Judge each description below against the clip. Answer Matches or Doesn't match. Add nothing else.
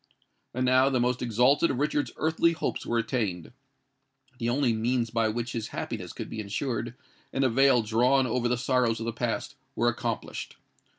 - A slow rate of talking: Doesn't match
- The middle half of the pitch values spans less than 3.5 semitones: Matches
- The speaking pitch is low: Matches